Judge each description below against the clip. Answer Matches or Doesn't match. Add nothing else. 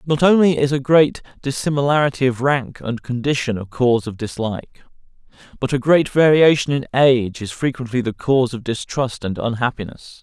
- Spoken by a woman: Doesn't match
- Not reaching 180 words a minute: Matches